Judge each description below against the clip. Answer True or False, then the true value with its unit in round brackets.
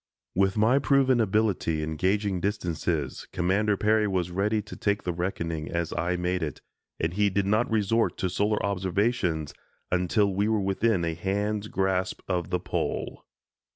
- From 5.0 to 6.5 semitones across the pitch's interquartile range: False (3.2 semitones)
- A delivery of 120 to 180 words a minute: True (160 wpm)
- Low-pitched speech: True (95 Hz)